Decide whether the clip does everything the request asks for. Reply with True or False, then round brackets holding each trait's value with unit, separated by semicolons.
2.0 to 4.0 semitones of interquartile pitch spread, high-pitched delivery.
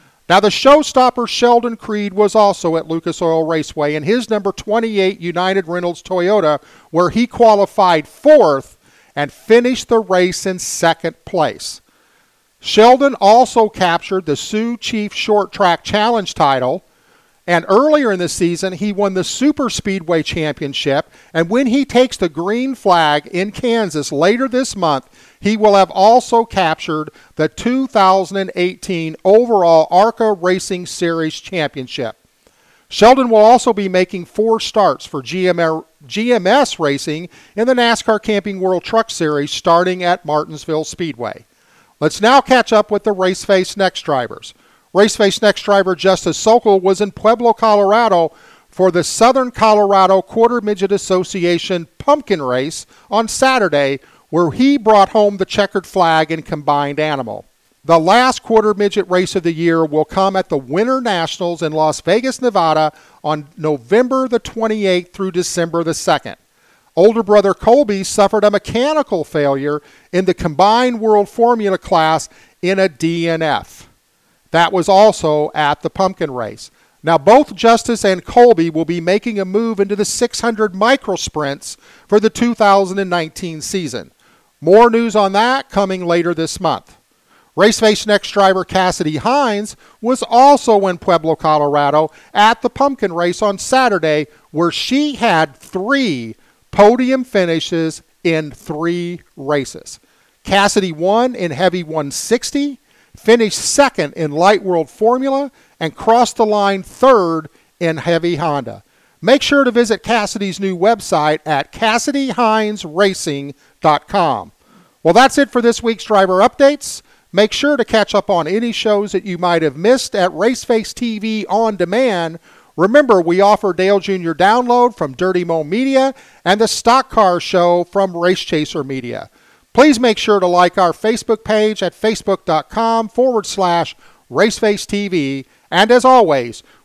False (5.1 semitones; 195 Hz)